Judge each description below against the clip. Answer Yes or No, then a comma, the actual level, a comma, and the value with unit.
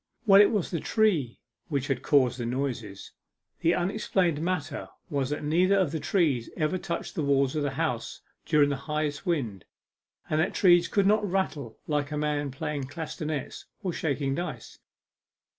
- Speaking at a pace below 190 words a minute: Yes, average, 170 wpm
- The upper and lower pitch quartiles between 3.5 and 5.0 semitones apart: Yes, average, 4.0 semitones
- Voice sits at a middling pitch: Yes, medium, 150 Hz